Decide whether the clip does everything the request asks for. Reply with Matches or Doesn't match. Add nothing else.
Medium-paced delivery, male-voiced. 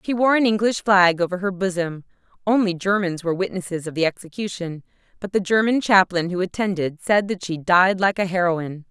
Doesn't match